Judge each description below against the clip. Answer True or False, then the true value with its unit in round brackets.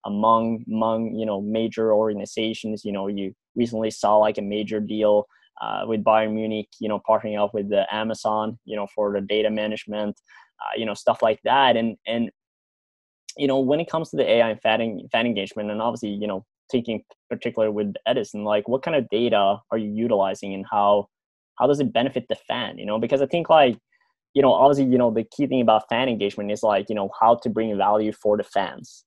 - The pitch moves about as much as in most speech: False (1.5 semitones)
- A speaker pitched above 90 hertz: True (110 Hz)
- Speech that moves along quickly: True (215 wpm)